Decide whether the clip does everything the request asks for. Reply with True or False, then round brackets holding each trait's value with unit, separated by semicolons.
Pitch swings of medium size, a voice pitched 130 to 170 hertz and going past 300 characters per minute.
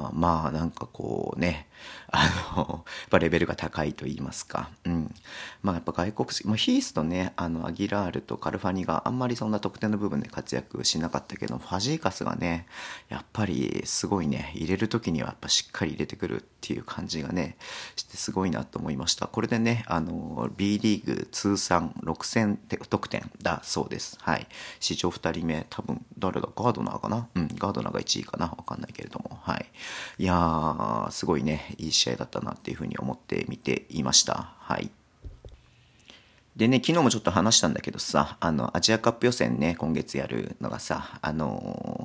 False (4.6 semitones; 90 Hz; 375 characters per minute)